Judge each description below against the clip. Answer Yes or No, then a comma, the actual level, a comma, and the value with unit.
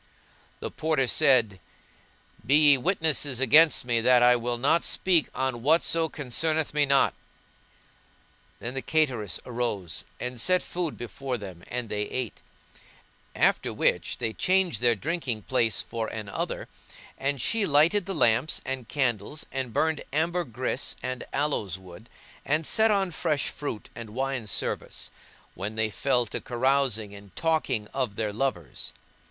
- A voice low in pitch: Yes, low, 130 Hz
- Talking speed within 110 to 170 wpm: Yes, average, 145 wpm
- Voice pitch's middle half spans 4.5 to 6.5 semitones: Yes, average, 5.2 semitones